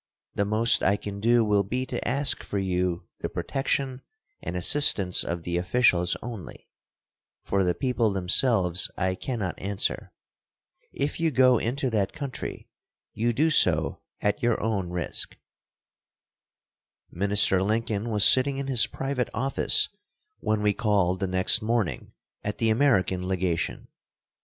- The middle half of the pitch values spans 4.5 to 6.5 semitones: Yes, average, 5.0 semitones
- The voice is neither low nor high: No, low, 105 Hz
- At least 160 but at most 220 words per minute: No, average, 140 wpm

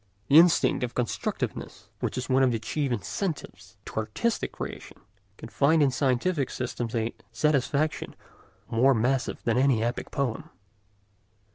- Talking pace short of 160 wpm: Yes, average, 140 wpm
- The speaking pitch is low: Yes, low, 130 Hz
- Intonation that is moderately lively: Yes, average, 3.5 semitones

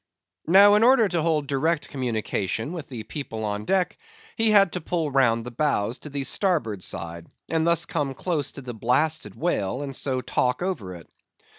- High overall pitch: No, medium, 140 Hz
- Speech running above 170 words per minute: Yes, average, 185 wpm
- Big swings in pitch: Yes, wide, 6.6 semitones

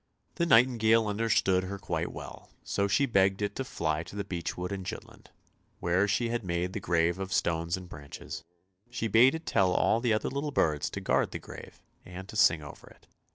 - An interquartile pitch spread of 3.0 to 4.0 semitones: No, average, 4.6 semitones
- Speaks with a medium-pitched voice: No, very low, 95 Hz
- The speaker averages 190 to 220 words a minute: Yes, fast, 205 wpm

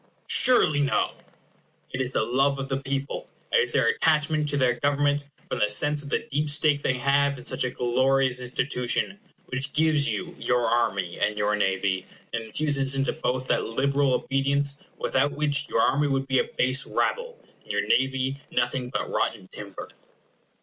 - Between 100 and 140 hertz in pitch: Yes, low, 135 Hz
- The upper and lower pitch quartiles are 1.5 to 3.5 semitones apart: Yes, narrow, 2.4 semitones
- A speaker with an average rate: Yes, average, 175 wpm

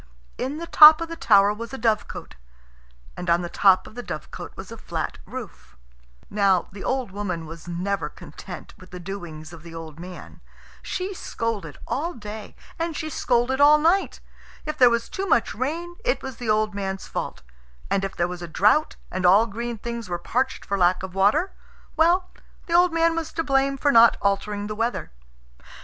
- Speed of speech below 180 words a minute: No, average, 195 wpm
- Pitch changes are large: Yes, wide, 7.7 semitones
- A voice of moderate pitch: No, high, 215 Hz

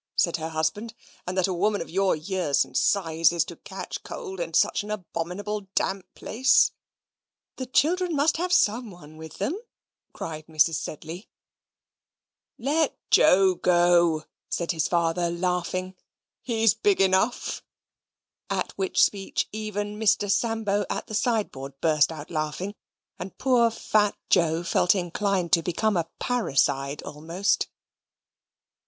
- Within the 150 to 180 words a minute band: No, slow, 135 wpm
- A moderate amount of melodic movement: Yes, average, 4.6 semitones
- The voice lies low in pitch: No, medium, 185 Hz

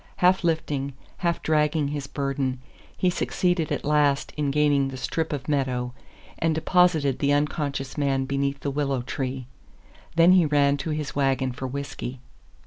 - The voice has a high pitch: No, medium, 140 Hz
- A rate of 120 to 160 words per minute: Yes, average, 155 wpm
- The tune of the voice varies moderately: No, narrow, 2.3 semitones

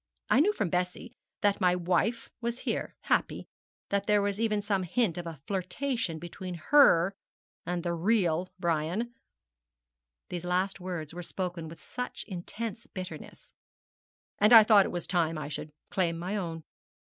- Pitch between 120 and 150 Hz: No, medium, 185 Hz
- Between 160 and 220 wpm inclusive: No, average, 150 wpm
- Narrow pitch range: No, average, 3.5 semitones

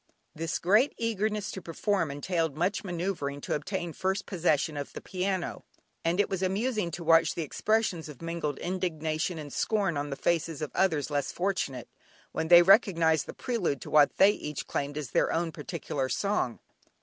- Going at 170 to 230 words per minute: Yes, average, 175 wpm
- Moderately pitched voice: Yes, medium, 170 Hz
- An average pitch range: Yes, average, 4.0 semitones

